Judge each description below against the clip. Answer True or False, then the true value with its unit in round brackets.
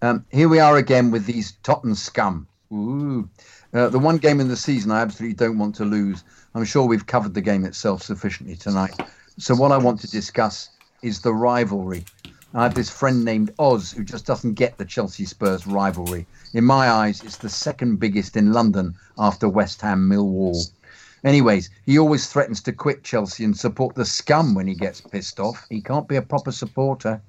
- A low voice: True (110 Hz)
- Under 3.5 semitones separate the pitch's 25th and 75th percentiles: False (4.4 semitones)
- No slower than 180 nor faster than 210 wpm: True (200 wpm)